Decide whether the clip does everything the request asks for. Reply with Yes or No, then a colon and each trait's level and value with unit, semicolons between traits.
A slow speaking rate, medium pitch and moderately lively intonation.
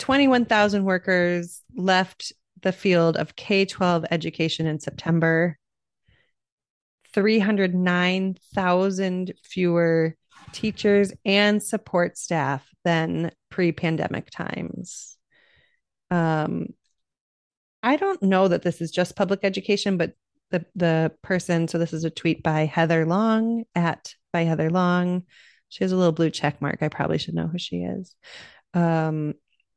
Yes: slow, 120 wpm; medium, 175 Hz; average, 3.0 semitones